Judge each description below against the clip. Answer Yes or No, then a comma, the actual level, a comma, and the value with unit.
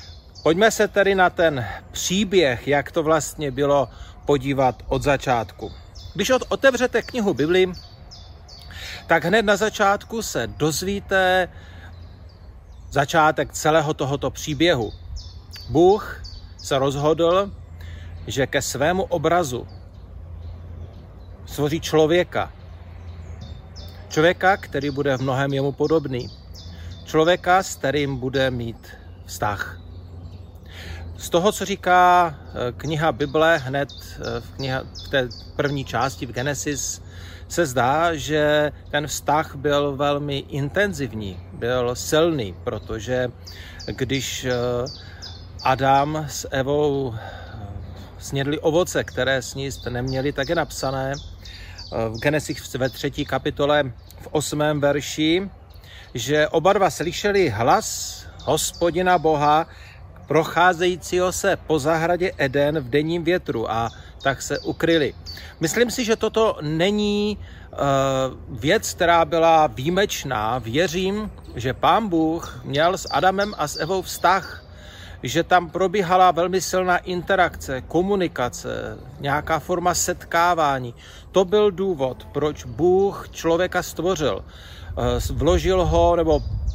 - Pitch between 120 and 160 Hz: Yes, medium, 140 Hz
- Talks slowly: Yes, slow, 110 wpm